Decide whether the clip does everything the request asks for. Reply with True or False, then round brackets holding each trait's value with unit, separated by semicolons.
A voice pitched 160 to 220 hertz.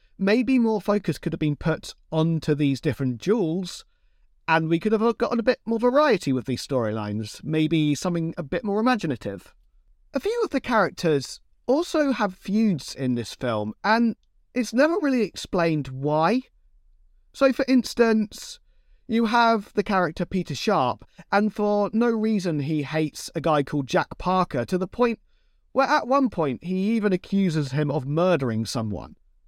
True (185 Hz)